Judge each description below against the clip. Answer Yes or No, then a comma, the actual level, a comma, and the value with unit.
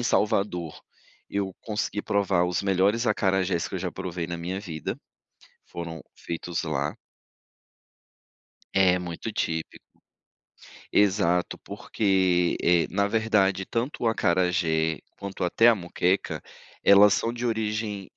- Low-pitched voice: Yes, very low, 95 Hz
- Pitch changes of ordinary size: Yes, average, 3.1 semitones